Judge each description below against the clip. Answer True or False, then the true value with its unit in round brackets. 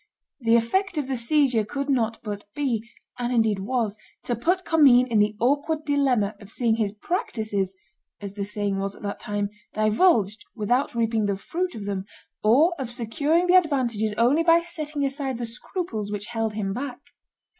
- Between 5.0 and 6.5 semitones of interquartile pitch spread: True (5.3 semitones)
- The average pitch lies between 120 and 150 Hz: False (235 Hz)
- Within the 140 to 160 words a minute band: False (175 wpm)